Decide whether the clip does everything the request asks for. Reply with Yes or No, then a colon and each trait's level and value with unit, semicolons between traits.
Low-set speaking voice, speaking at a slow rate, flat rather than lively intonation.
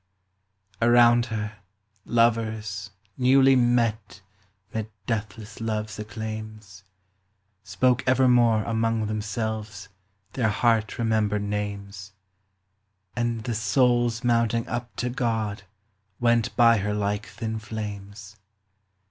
Yes: low, 110 Hz; slow, 95 wpm; narrow, 2.1 semitones